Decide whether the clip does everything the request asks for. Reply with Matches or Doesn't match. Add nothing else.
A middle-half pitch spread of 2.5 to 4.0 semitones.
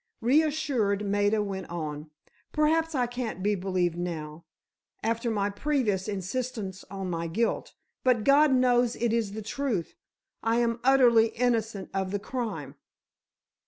Doesn't match